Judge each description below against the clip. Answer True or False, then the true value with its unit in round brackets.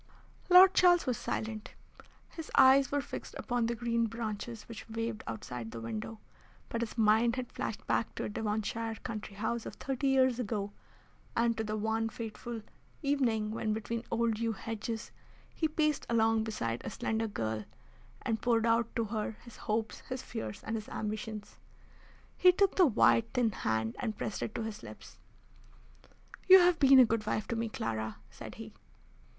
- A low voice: False (225 Hz)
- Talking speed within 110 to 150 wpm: False (175 wpm)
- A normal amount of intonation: False (2.1 semitones)